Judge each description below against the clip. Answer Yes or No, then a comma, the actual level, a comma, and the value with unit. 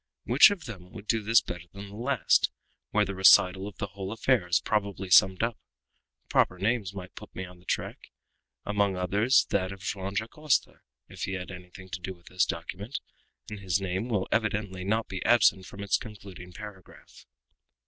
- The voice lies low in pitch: Yes, low, 100 Hz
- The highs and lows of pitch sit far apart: No, narrow, 2.5 semitones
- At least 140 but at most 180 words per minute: No, average, 190 wpm